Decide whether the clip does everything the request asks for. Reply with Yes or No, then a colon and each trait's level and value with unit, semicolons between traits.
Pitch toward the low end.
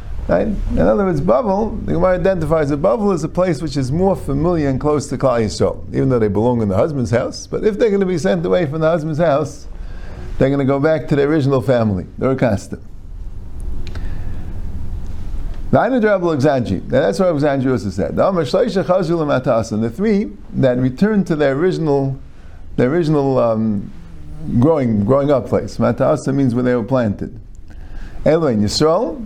Yes: low, 130 Hz